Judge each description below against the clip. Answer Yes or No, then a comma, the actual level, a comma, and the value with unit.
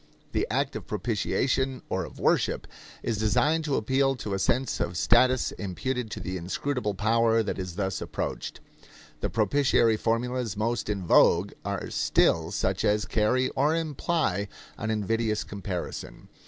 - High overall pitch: No, low, 110 Hz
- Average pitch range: Yes, average, 4.1 semitones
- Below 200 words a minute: Yes, average, 150 wpm